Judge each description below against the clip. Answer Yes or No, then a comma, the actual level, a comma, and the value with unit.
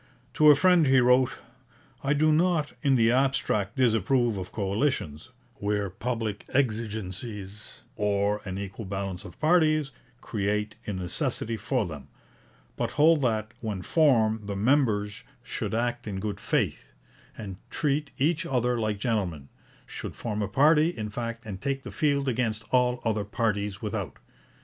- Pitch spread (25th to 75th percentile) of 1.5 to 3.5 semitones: No, average, 4.7 semitones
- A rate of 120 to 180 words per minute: Yes, average, 150 wpm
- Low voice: Yes, low, 110 Hz